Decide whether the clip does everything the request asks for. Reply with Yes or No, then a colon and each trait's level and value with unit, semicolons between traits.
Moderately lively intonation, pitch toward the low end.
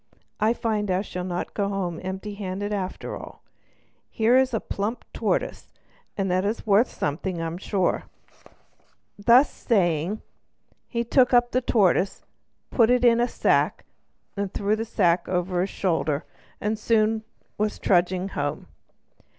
No: average, 3.6 semitones; high, 200 Hz